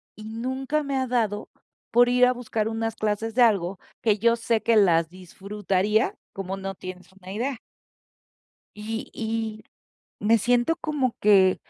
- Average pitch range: Yes, average, 3.4 semitones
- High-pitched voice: Yes, high, 220 Hz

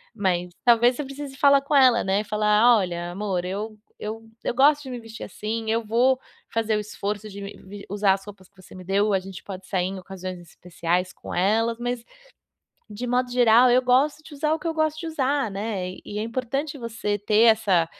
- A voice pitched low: No, high, 215 Hz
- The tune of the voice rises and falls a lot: No, average, 4.4 semitones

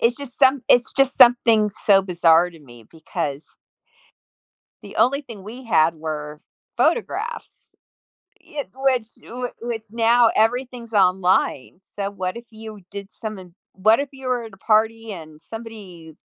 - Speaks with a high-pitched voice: Yes, high, 220 Hz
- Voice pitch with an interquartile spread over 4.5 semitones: Yes, average, 5.2 semitones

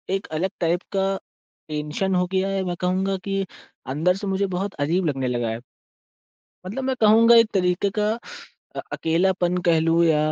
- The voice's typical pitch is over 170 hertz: Yes, medium, 185 Hz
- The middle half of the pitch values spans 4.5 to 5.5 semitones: No, average, 2.9 semitones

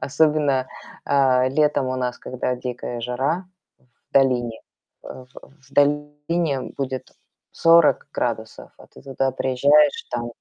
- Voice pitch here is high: No, low, 135 Hz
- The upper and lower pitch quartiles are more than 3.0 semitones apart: No, narrow, 2.5 semitones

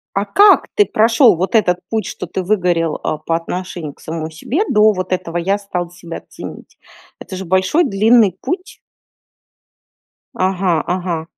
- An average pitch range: Yes, average, 3.9 semitones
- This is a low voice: No, medium, 185 Hz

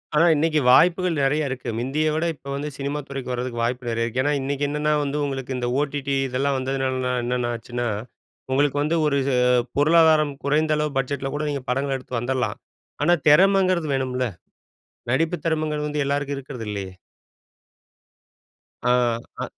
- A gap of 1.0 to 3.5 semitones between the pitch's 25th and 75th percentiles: Yes, average, 2.9 semitones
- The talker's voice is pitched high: No, medium, 140 Hz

